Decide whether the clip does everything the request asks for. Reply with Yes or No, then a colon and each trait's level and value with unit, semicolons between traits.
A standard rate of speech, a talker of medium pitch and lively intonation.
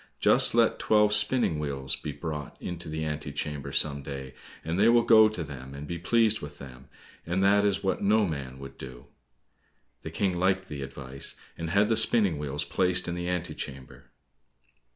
No: average, 190 wpm; very low, 80 Hz; wide, 6.0 semitones